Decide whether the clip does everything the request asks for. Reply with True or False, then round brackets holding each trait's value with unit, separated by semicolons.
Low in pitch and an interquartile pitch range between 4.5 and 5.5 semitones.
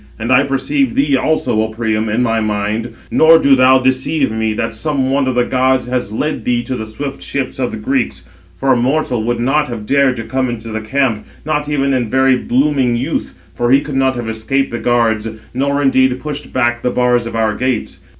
False (125 Hz; 3.0 semitones)